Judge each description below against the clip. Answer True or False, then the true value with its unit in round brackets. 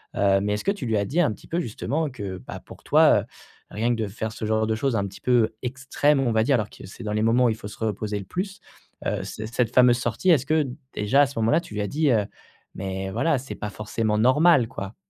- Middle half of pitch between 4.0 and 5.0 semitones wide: True (4.4 semitones)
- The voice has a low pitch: True (115 Hz)